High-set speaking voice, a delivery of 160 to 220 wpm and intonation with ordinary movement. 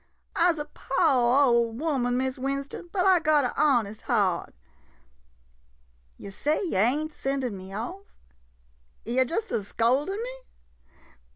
No: very high, 270 Hz; slow, 135 wpm; average, 4.7 semitones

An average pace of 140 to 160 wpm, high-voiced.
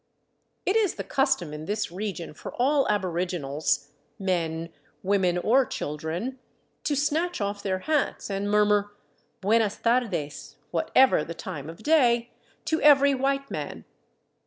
Yes: average, 155 wpm; high, 205 Hz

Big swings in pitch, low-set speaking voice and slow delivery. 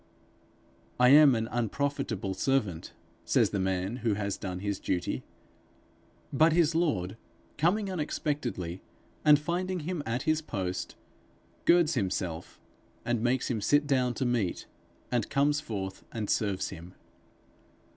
Yes: wide, 7.5 semitones; low, 120 Hz; slow, 130 wpm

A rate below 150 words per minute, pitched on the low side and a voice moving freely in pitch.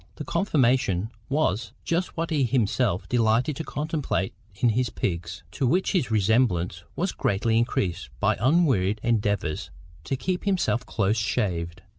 Yes: average, 140 wpm; low, 115 Hz; wide, 6.2 semitones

